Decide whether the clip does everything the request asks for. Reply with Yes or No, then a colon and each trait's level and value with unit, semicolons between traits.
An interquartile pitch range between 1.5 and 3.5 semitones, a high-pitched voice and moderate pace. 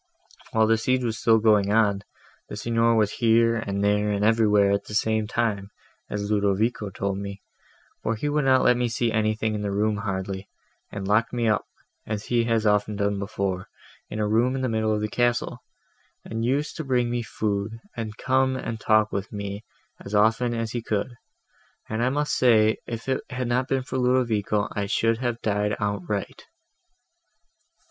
No: narrow, 2.4 semitones; low, 110 Hz; average, 180 wpm